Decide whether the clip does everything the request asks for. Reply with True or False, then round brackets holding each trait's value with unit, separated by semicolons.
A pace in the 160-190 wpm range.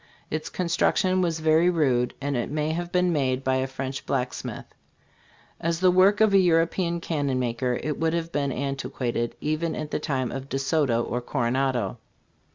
True (185 wpm)